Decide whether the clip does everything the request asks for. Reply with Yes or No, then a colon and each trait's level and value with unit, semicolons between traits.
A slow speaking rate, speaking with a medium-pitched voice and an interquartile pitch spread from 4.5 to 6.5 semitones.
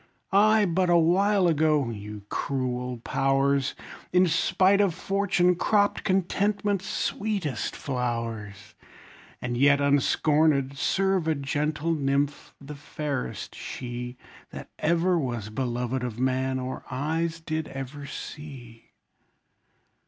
Yes: slow, 110 wpm; medium, 145 Hz; average, 5.3 semitones